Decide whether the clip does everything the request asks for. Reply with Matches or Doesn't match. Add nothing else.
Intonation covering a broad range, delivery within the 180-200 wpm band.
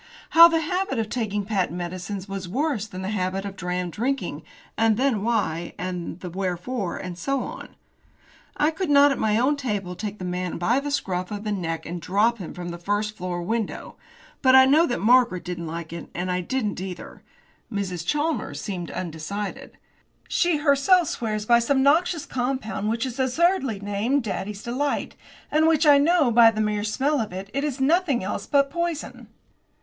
Matches